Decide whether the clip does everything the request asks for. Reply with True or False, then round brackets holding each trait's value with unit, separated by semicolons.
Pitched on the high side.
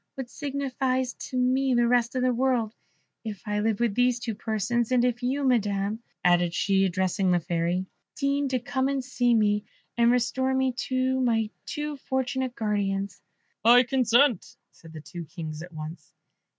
True (240 Hz)